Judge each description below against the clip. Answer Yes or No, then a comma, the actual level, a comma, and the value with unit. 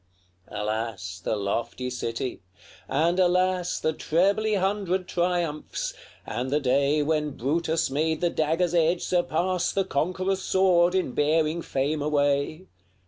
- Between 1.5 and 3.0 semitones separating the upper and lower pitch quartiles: No, average, 4.3 semitones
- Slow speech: Yes, slow, 130 wpm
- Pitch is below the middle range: No, medium, 160 Hz